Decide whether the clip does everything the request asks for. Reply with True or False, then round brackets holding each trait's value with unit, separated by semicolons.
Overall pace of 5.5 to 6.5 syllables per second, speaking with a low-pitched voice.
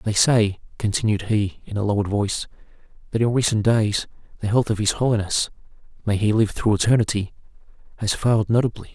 True (6.0 syllables/s; 110 Hz)